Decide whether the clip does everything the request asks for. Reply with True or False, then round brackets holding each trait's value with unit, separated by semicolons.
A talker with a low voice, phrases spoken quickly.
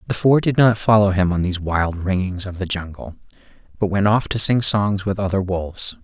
True (100 Hz; 220 wpm)